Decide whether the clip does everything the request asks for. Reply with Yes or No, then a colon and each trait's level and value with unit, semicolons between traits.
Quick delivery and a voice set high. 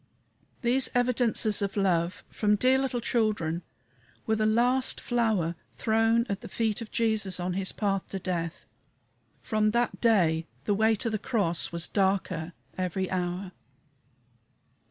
No: average, 140 wpm; high, 210 Hz